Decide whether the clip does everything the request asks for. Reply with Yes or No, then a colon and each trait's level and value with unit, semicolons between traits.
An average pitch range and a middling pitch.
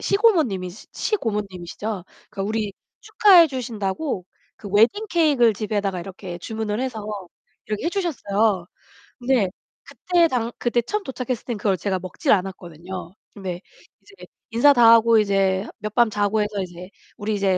No: average, 4.7 semitones; high, 215 Hz